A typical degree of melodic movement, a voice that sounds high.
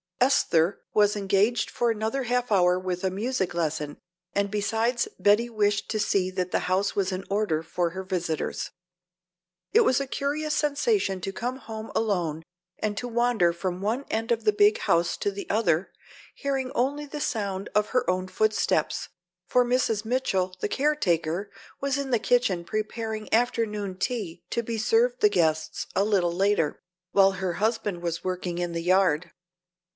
Yes: average, 4.6 semitones; high, 205 Hz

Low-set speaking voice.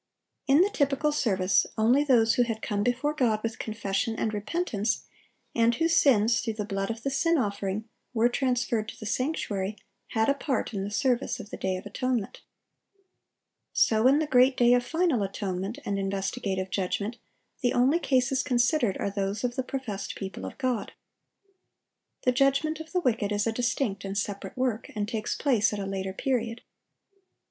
No: high, 230 Hz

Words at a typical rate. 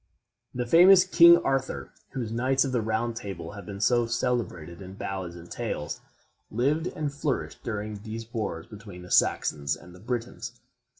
Yes: average, 165 wpm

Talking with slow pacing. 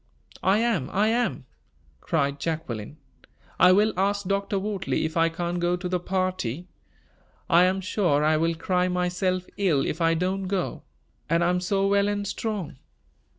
No: average, 165 wpm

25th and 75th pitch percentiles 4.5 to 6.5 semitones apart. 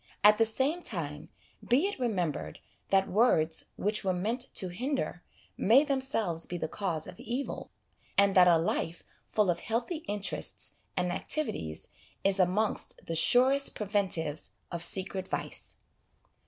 Yes: wide, 5.5 semitones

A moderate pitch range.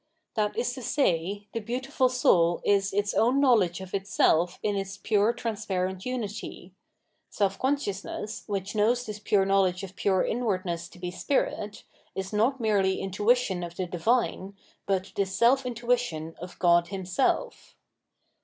Yes: average, 3.9 semitones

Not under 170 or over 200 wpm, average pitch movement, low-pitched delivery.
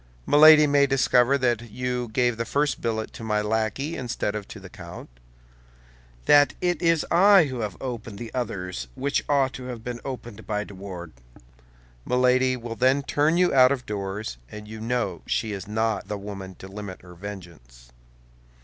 Yes: average, 175 wpm; average, 4.3 semitones; low, 115 Hz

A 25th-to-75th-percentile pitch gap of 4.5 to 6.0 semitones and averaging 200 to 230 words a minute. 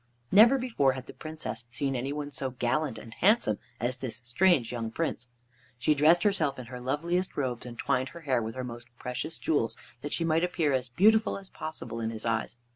Yes: average, 5.2 semitones; fast, 205 wpm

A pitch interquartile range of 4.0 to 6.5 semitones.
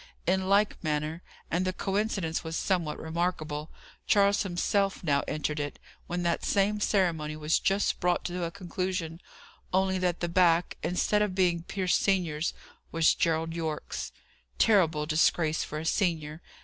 No: average, 3.0 semitones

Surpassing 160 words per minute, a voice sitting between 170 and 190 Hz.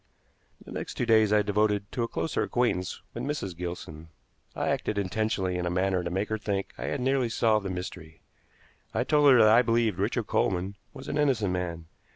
No: average, 200 wpm; low, 105 Hz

